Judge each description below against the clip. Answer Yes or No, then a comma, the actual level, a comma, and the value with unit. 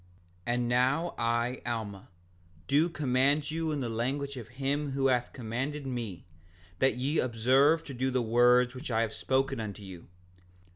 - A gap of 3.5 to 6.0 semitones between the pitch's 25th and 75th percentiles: No, average, 3.0 semitones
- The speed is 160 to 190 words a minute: Yes, average, 165 wpm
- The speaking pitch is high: No, low, 130 Hz